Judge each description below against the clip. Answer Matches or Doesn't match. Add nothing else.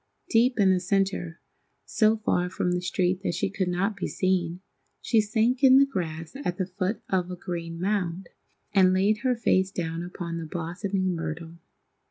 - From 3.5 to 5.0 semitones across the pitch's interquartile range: Doesn't match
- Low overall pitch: Doesn't match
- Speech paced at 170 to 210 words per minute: Matches